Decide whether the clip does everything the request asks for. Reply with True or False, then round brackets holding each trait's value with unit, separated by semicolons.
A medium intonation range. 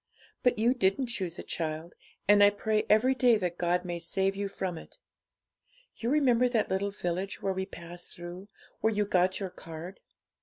True (3.6 semitones)